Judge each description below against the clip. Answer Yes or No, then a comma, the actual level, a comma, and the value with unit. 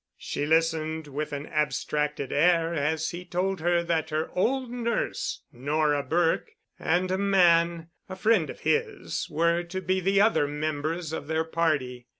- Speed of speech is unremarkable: Yes, average, 160 wpm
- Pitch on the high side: No, medium, 165 Hz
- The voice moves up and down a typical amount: Yes, average, 3.0 semitones